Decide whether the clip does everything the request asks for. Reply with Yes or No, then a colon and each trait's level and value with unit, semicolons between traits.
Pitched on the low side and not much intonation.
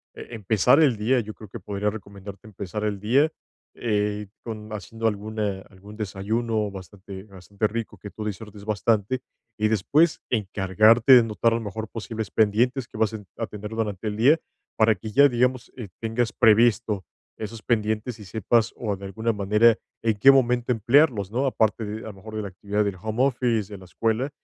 Yes: low, 110 Hz; narrow, 2.1 semitones